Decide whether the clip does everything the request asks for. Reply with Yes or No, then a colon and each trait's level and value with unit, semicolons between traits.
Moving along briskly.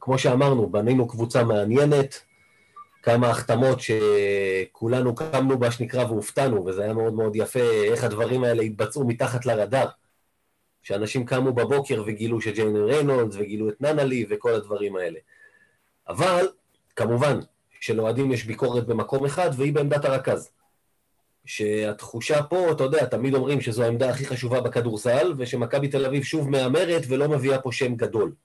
No: average, 140 wpm